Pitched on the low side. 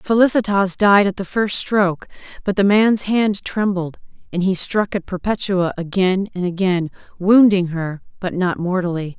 No: high, 190 Hz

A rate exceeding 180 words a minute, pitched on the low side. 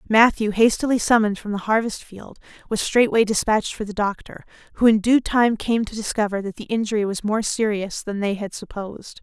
No: average, 195 wpm; high, 215 Hz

